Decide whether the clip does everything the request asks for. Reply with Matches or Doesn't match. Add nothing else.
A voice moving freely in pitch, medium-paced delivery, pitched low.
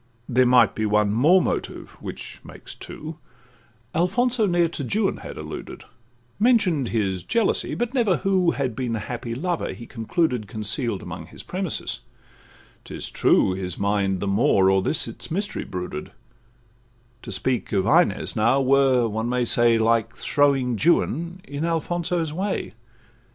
Matches